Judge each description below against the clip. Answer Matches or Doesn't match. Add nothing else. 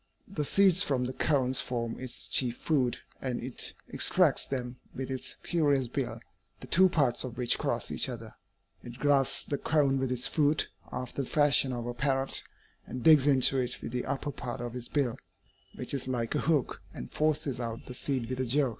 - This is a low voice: Matches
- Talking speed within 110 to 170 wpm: Doesn't match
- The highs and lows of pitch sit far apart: Doesn't match